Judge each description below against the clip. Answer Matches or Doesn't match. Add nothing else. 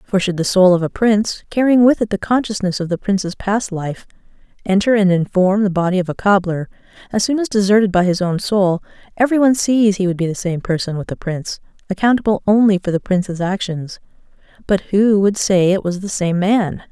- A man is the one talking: Doesn't match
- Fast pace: Matches